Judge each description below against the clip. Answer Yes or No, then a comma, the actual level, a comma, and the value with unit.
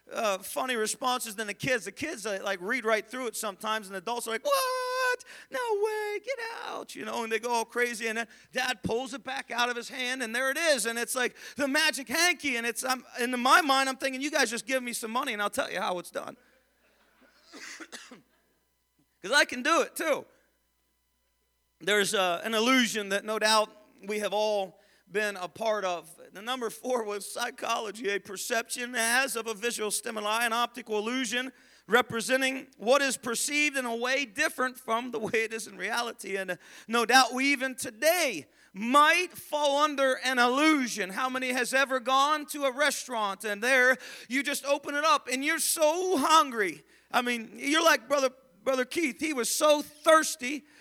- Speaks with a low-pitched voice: No, very high, 250 Hz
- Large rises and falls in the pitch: No, average, 4.1 semitones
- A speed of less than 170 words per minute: No, average, 195 wpm